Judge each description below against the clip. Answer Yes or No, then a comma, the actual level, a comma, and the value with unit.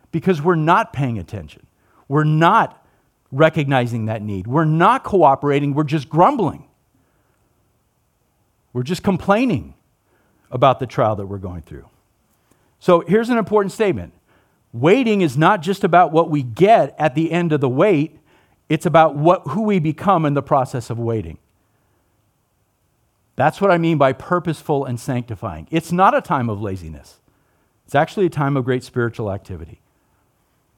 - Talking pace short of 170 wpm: Yes, average, 150 wpm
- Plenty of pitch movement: Yes, wide, 7.2 semitones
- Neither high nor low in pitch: Yes, medium, 145 Hz